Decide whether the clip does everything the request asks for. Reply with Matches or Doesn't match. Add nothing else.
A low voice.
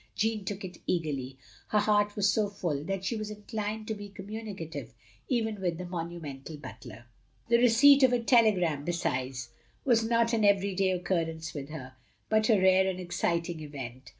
Doesn't match